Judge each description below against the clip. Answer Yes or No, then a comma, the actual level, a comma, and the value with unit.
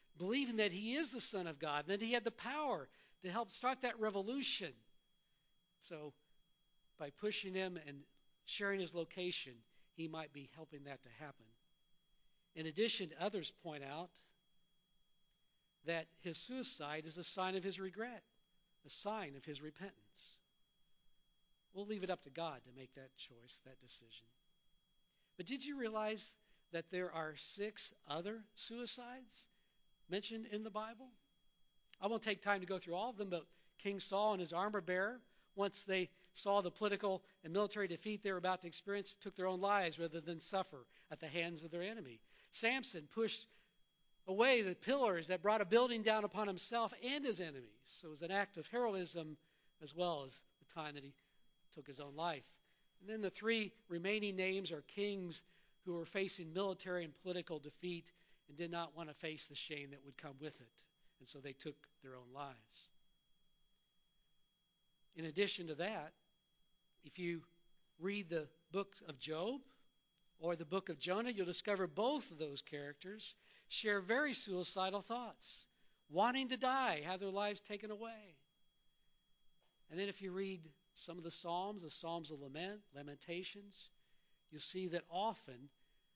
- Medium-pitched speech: Yes, medium, 180 Hz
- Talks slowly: No, average, 170 wpm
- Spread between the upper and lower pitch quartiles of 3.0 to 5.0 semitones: Yes, average, 4.3 semitones